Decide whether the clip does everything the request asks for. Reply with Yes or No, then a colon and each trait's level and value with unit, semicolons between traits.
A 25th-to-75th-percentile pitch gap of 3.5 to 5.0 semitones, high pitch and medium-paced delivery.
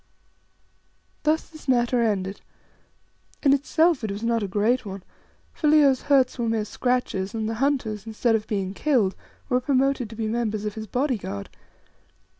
Yes: average, 4.0 semitones; high, 230 Hz; average, 165 wpm